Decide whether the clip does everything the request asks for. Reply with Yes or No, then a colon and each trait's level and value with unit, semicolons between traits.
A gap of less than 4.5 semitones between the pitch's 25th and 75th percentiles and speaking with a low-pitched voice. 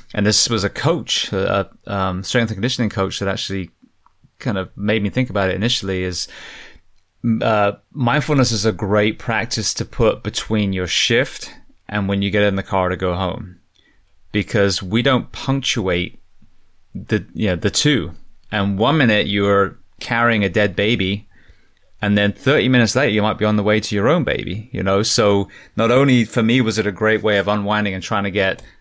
Yes: average, 2.8 semitones; low, 105 Hz